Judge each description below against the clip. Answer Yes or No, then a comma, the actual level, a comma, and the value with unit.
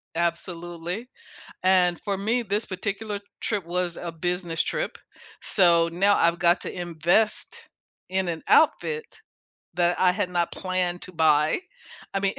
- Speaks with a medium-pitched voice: Yes, medium, 180 Hz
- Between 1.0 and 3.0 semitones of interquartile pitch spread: Yes, narrow, 2.4 semitones